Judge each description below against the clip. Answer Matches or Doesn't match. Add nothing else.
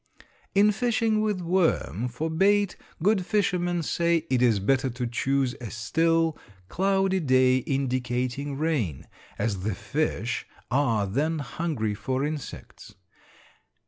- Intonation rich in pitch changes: Matches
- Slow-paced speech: Matches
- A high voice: Doesn't match